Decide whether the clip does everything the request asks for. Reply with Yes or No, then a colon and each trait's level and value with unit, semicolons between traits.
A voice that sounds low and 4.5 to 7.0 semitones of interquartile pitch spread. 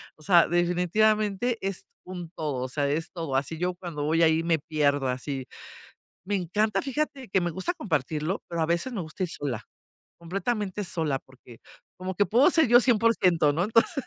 No: medium, 175 Hz; average, 5.2 semitones